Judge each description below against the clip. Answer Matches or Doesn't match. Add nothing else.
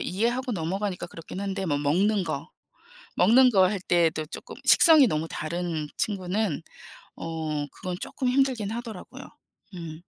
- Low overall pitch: Doesn't match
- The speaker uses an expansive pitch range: Doesn't match